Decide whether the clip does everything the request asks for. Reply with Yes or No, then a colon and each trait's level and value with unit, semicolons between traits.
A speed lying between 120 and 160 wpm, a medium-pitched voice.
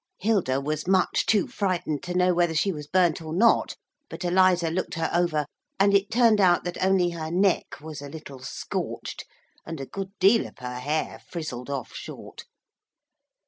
No: average, 180 wpm; medium, 175 Hz